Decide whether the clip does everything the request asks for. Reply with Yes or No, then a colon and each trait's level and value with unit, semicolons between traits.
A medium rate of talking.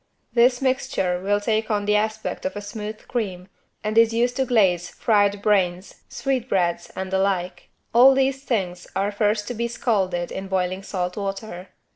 Yes: average, 170 wpm